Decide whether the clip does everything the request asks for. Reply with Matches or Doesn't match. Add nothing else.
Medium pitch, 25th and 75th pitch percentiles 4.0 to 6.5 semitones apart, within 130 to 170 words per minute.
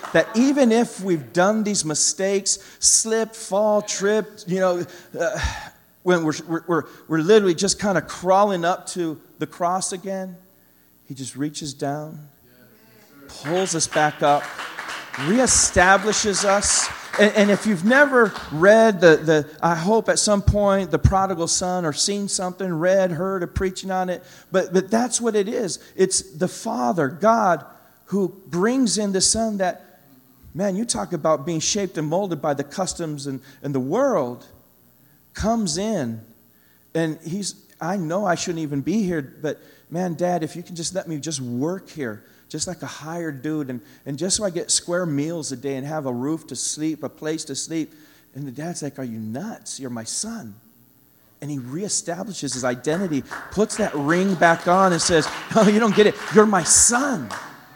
Doesn't match